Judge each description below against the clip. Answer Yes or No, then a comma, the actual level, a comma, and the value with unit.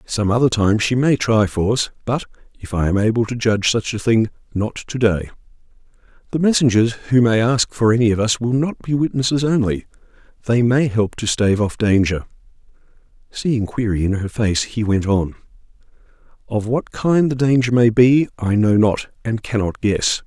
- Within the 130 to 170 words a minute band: No, average, 180 wpm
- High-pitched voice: No, low, 115 Hz